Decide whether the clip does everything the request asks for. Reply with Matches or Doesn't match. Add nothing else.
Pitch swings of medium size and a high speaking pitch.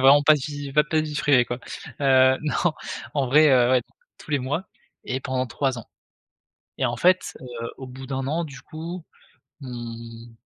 Doesn't match